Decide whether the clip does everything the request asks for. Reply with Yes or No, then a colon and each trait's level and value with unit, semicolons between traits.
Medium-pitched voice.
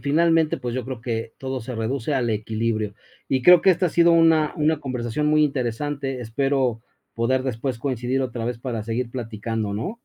No: low, 130 Hz